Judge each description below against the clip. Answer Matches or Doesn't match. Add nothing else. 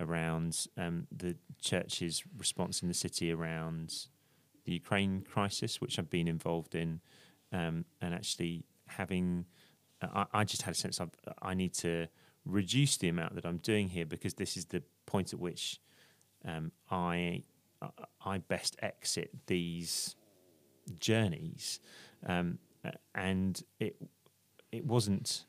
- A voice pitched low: Matches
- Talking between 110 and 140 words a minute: Matches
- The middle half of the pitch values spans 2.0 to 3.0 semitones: Matches